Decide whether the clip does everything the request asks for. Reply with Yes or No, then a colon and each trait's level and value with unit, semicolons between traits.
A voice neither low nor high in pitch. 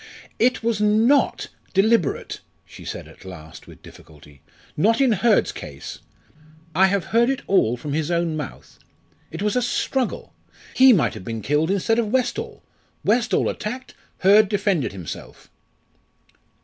No: high, 205 Hz